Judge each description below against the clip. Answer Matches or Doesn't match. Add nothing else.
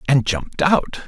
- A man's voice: Matches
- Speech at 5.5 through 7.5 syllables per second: Matches